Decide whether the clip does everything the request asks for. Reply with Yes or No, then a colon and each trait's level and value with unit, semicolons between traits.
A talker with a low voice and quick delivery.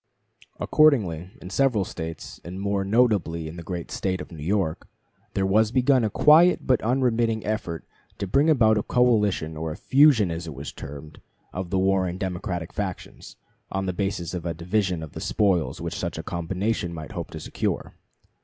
No: very low, 95 Hz; average, 180 wpm